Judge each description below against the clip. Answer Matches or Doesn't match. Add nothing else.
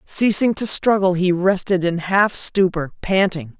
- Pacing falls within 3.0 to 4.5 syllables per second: Matches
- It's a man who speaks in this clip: Doesn't match